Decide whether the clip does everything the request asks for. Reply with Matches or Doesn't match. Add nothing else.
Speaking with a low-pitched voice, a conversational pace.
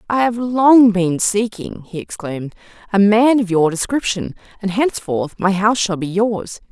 Doesn't match